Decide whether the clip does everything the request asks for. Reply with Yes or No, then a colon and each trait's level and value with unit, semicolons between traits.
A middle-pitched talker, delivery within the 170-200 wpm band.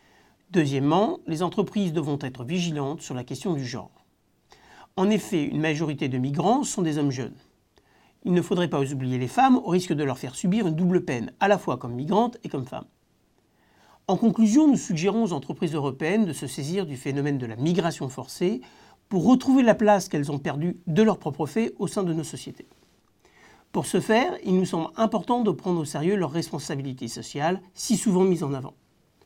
Yes: medium, 170 Hz; average, 195 wpm